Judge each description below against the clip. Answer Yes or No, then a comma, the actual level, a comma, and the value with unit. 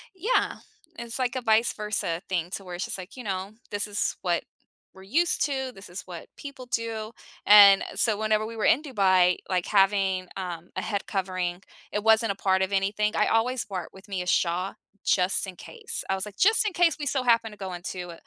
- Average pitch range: Yes, average, 3.6 semitones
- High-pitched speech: Yes, high, 200 Hz